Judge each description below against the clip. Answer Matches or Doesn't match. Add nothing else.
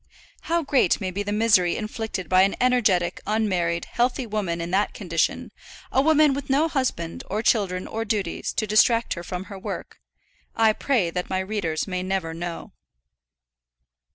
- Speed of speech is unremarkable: Matches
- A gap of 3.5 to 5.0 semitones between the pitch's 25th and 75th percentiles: Matches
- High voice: Matches